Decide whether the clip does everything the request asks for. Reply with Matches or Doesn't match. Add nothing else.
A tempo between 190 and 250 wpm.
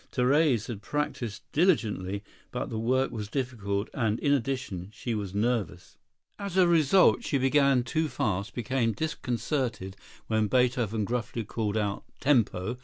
Doesn't match